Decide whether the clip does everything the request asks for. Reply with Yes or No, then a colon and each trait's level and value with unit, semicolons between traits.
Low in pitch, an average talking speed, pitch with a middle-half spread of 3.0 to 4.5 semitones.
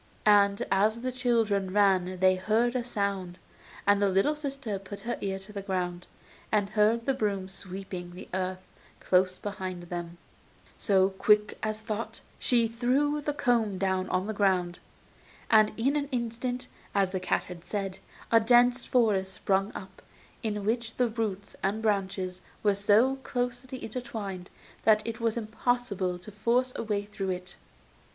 No: high, 205 Hz; average, 160 wpm; average, 3.6 semitones